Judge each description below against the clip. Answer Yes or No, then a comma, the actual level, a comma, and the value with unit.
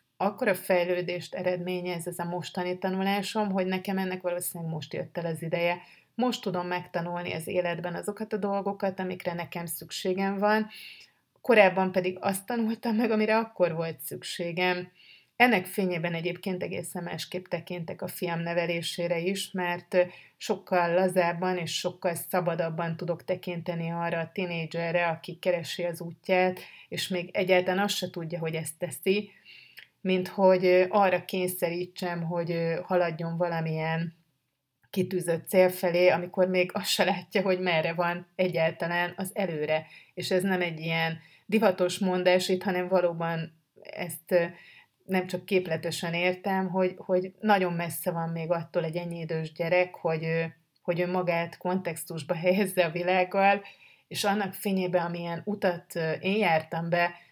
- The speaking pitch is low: No, medium, 180 Hz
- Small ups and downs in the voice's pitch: Yes, narrow, 1.6 semitones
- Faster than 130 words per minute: Yes, average, 140 wpm